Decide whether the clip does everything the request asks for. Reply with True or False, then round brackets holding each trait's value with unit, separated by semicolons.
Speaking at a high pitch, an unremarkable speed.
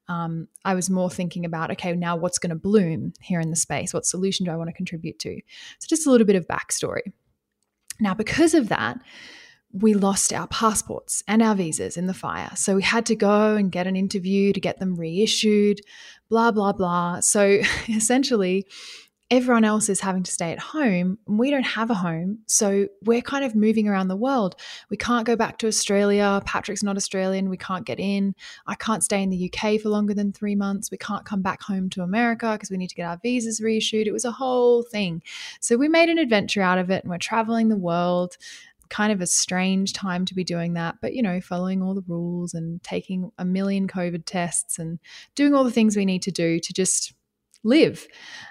False (200 Hz; 215 wpm)